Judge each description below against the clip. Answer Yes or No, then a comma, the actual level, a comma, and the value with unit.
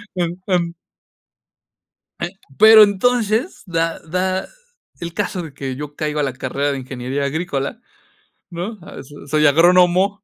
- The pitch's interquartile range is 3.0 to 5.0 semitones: Yes, average, 4.6 semitones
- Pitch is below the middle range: No, medium, 170 Hz